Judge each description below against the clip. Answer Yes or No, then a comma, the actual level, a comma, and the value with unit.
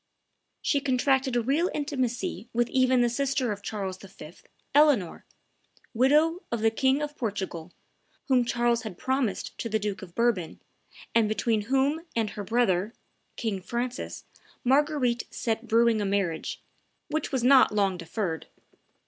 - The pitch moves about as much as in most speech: Yes, average, 4.2 semitones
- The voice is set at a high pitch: Yes, high, 235 Hz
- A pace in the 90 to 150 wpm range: Yes, average, 145 wpm